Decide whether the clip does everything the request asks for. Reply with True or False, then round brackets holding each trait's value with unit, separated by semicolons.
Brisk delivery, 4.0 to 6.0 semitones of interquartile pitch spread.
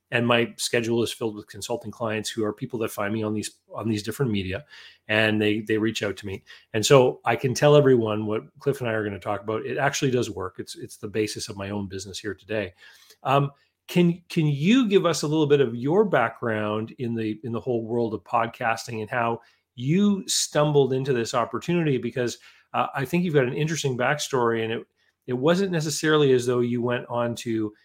True (220 wpm; 4.4 semitones)